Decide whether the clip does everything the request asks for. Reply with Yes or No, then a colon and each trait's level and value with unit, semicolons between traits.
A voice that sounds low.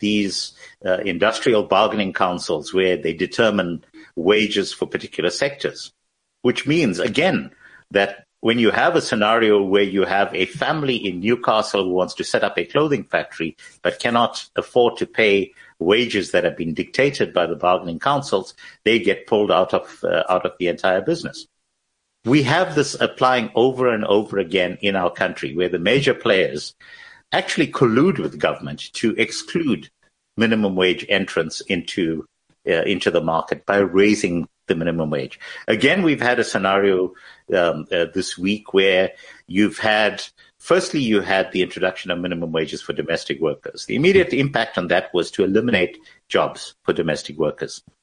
Yes: low, 100 Hz